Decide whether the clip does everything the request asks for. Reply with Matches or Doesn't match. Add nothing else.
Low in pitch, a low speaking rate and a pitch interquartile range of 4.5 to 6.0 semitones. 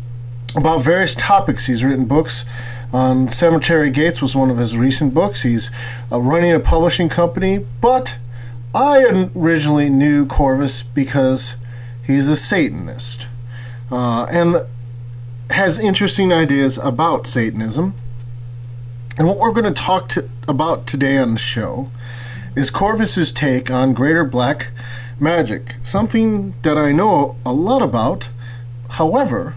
Matches